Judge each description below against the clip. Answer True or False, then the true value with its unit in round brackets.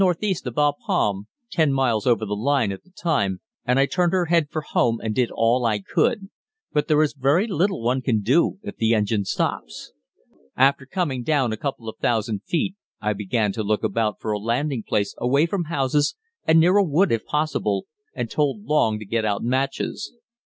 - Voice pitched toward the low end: True (130 Hz)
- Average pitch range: False (6.3 semitones)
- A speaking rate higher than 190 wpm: True (200 wpm)